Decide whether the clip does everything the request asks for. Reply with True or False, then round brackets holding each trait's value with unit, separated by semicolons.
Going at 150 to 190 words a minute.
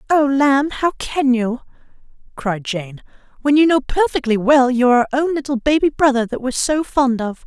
True (185 wpm)